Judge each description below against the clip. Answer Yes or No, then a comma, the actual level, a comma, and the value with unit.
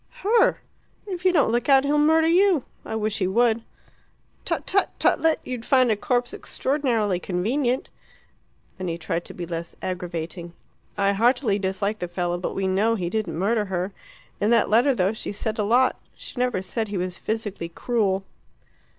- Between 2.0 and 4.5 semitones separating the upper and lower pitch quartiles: No, average, 5.2 semitones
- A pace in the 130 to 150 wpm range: No, average, 175 wpm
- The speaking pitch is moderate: No, high, 215 Hz